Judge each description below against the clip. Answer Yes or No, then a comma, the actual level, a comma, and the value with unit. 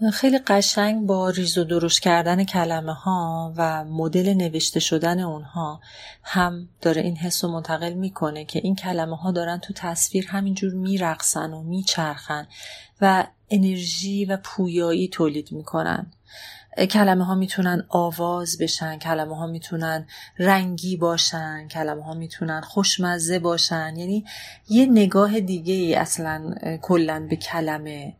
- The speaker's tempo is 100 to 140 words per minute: Yes, average, 130 wpm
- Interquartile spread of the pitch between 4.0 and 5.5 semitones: No, narrow, 2.6 semitones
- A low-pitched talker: No, medium, 175 Hz